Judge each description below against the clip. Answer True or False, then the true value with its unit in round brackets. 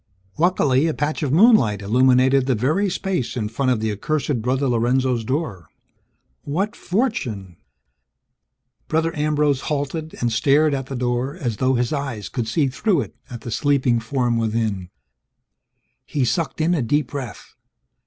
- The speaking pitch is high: False (130 Hz)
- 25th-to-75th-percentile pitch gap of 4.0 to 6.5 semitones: True (4.4 semitones)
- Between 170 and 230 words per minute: False (155 wpm)